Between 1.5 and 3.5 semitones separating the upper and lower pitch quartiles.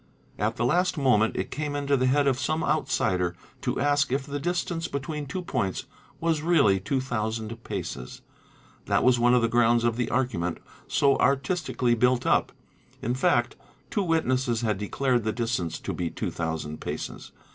No: average, 4.1 semitones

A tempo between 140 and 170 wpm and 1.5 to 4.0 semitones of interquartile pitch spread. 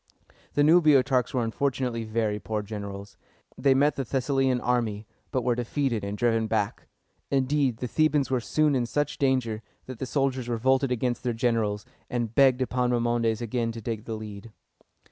Yes: average, 165 wpm; average, 2.9 semitones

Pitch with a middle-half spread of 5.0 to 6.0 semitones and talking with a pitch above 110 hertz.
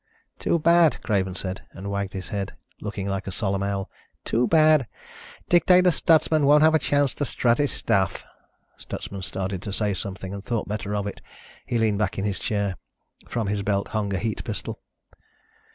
No: wide, 5.6 semitones; low, 105 Hz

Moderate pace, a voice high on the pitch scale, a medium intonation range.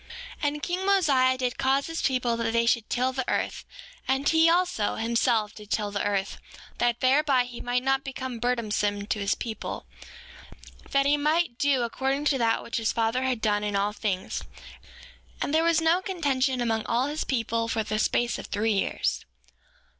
Yes: average, 185 wpm; very high, 250 Hz; average, 3.9 semitones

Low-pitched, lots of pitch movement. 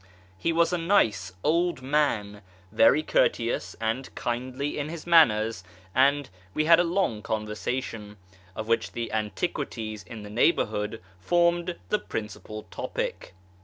Yes: low, 120 Hz; wide, 7.3 semitones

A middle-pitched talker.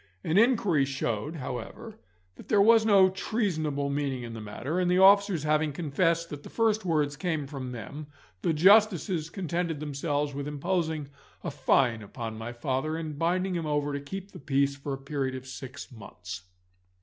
Yes: medium, 150 Hz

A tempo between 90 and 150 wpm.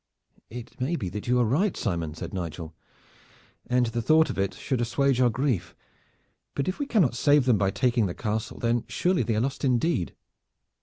No: average, 195 wpm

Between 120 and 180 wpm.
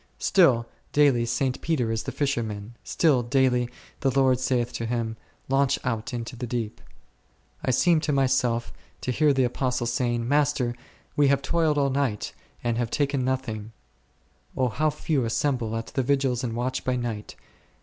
Yes: average, 170 wpm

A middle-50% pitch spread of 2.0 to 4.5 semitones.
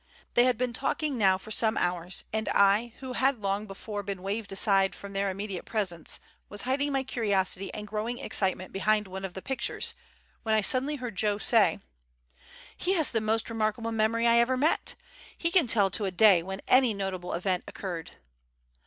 Yes: average, 3.5 semitones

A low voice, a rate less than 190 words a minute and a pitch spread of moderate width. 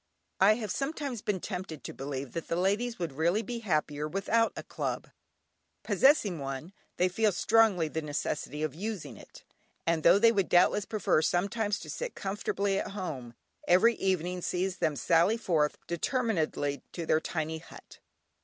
No: medium, 180 Hz; average, 165 wpm; average, 5.0 semitones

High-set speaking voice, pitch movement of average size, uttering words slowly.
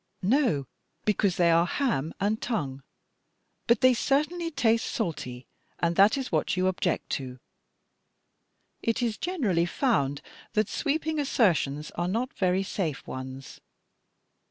No: high, 195 Hz; wide, 7.4 semitones; slow, 130 wpm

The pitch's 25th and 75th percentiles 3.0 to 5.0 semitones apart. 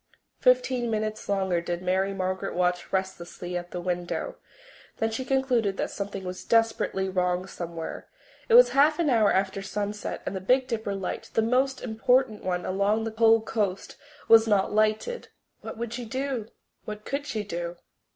Yes: average, 3.7 semitones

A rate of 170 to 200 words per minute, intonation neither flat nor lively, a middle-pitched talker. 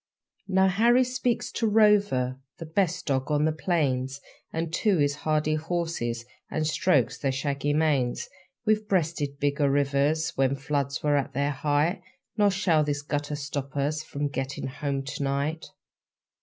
No: average, 155 wpm; average, 3.3 semitones; medium, 150 Hz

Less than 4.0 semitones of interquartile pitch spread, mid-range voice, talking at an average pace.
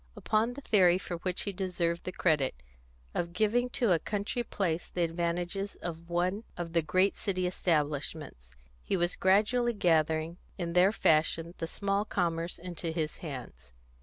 Yes: average, 3.2 semitones; medium, 175 Hz; average, 160 wpm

